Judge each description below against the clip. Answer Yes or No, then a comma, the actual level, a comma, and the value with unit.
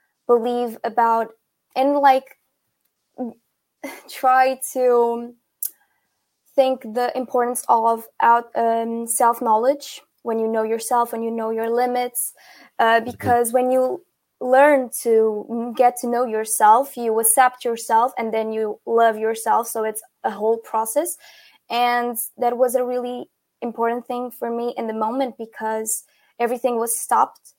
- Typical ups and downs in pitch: No, narrow, 1.9 semitones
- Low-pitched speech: No, high, 240 Hz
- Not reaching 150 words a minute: Yes, slow, 135 wpm